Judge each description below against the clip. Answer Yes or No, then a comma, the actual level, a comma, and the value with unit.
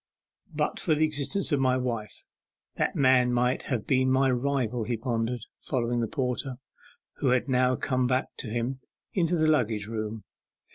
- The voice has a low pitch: Yes, low, 125 Hz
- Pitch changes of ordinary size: No, narrow, 2.2 semitones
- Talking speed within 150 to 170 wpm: Yes, average, 165 wpm